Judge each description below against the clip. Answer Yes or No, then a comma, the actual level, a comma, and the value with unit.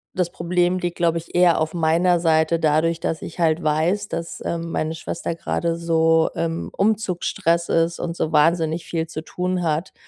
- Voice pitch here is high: No, medium, 165 Hz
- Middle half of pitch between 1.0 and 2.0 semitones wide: Yes, narrow, 1.4 semitones